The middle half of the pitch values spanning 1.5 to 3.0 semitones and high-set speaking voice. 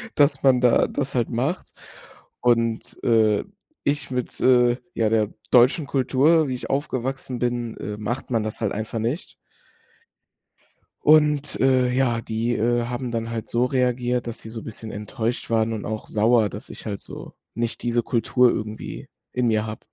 No: narrow, 2.4 semitones; low, 120 Hz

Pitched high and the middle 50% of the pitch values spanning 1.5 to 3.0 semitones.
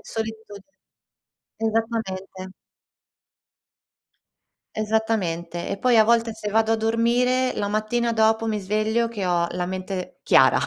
Yes: high, 220 Hz; narrow, 2.6 semitones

